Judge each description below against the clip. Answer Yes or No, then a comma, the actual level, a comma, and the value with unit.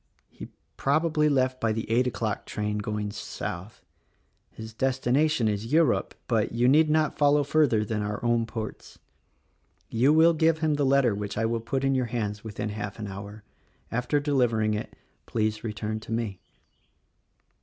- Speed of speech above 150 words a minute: Yes, average, 165 wpm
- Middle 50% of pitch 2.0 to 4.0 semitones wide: No, average, 4.5 semitones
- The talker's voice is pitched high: No, low, 115 Hz